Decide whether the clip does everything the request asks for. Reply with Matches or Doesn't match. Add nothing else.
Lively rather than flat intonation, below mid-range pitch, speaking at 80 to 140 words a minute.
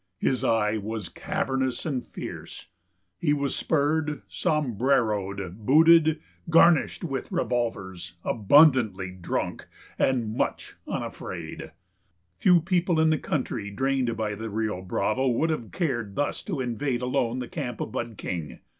Matches